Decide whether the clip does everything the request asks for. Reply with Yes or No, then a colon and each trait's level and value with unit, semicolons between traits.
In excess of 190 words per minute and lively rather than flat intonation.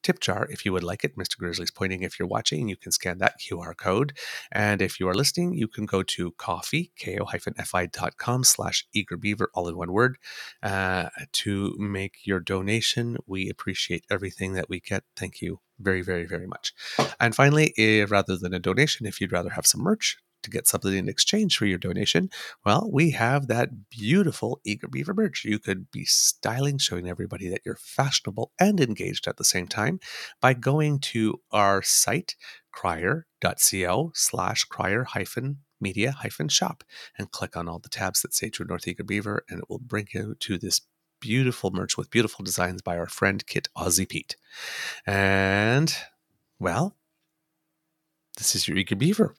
No: average, 180 wpm; wide, 6.7 semitones